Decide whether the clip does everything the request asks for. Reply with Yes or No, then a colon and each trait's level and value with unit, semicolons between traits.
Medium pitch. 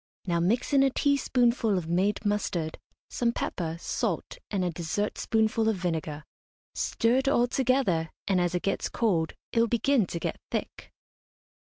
No: high, 205 Hz